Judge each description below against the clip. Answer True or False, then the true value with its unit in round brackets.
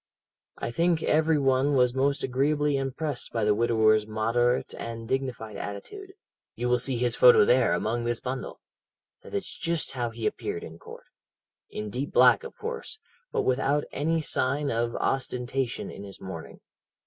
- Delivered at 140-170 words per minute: True (160 wpm)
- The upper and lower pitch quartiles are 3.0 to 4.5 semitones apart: True (3.7 semitones)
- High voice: False (125 Hz)